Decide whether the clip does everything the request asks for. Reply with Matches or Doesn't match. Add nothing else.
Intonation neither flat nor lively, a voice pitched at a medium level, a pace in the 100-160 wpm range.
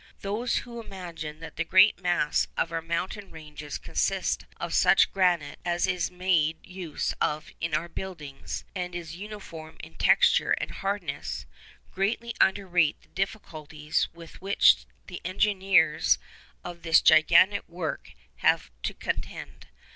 Matches